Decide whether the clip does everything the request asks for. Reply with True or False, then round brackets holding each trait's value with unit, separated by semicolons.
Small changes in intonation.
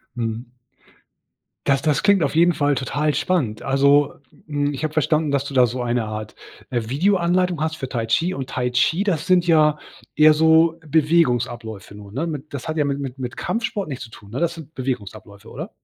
False (4.5 semitones)